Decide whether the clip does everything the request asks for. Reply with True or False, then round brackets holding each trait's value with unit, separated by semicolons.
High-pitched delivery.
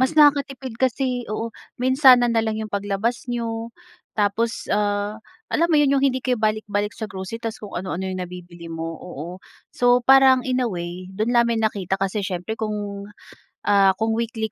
True (220 Hz)